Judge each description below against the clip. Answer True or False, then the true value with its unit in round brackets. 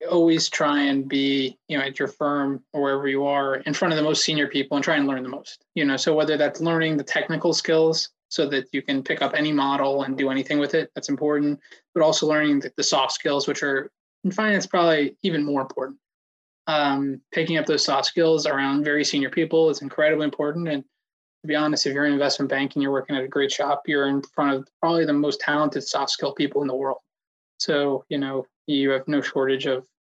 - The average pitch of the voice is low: False (145 Hz)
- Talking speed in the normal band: False (230 wpm)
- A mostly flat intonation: True (2.0 semitones)